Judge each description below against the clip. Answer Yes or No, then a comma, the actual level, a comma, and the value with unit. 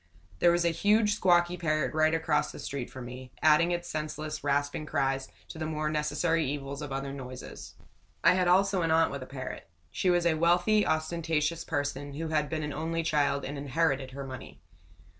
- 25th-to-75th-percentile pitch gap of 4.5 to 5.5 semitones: No, average, 3.1 semitones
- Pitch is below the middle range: No, medium, 155 Hz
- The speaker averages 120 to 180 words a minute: No, average, 195 wpm